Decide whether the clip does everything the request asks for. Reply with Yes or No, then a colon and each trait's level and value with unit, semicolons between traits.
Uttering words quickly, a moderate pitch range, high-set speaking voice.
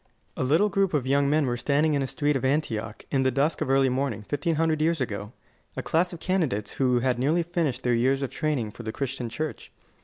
No: fast, 235 wpm; average, 3.8 semitones; medium, 140 Hz